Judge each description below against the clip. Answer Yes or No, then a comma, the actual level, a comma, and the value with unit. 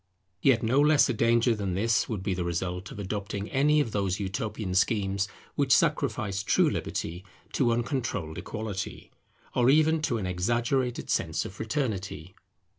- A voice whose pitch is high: No, low, 110 Hz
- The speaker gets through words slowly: No, average, 155 wpm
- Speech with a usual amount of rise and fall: Yes, average, 4.1 semitones